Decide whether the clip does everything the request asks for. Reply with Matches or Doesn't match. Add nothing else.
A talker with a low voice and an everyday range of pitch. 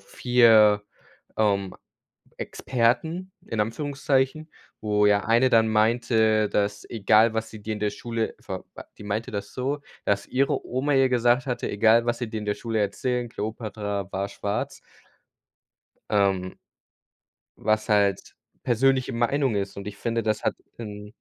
Matches